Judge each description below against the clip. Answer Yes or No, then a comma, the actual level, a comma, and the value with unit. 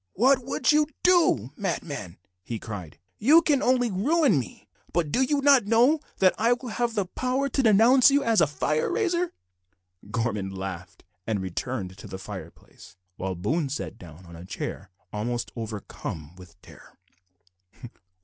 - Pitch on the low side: No, medium, 175 Hz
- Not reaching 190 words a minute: Yes, average, 160 wpm